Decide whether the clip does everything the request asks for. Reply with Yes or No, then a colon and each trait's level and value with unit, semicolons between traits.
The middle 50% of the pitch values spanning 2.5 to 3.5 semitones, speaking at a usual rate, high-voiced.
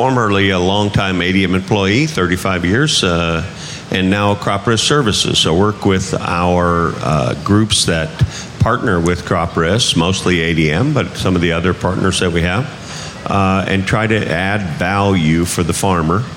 No: average, 2.9 semitones; average, 160 wpm; very low, 95 Hz